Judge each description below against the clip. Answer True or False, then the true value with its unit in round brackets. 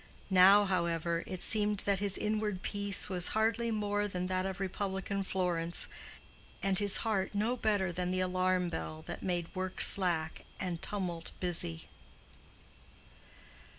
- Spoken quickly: False (140 wpm)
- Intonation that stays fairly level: True (2.3 semitones)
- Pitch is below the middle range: False (190 Hz)